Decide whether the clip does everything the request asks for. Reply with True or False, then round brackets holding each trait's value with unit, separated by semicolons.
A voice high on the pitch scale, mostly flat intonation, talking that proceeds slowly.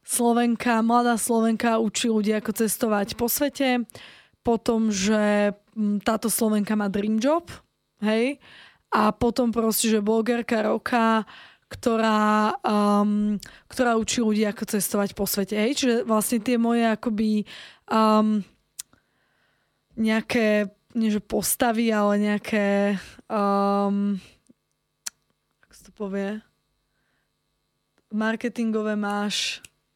True (220 Hz; 2.1 semitones; 100 wpm)